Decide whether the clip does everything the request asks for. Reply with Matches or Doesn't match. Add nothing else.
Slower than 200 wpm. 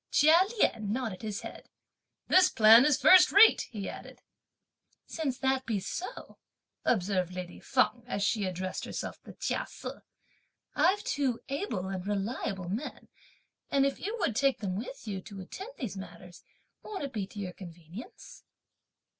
Matches